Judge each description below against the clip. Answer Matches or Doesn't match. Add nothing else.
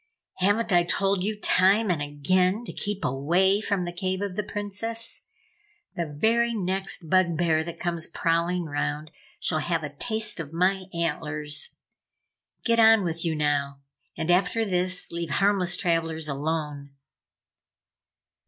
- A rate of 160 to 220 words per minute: Doesn't match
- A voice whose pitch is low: Doesn't match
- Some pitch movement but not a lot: Matches